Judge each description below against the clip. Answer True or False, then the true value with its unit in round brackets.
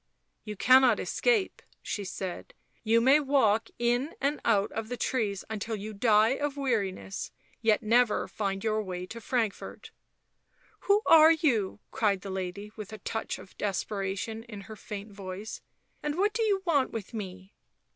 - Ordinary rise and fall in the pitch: True (4.5 semitones)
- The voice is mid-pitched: False (220 Hz)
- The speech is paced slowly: False (165 wpm)